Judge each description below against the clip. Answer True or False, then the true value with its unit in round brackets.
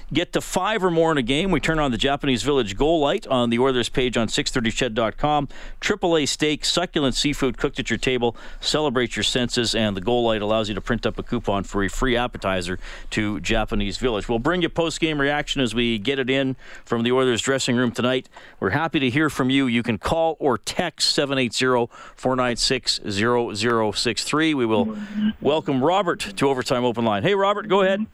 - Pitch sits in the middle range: False (130 Hz)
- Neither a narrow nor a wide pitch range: True (4.0 semitones)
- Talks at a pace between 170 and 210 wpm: True (205 wpm)